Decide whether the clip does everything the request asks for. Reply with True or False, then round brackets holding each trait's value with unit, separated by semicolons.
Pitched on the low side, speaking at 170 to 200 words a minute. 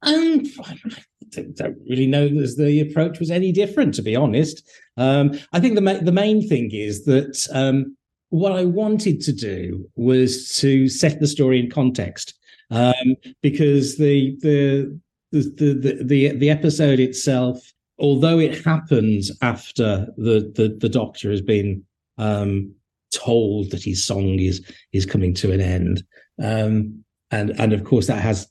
False (130 Hz; 160 wpm)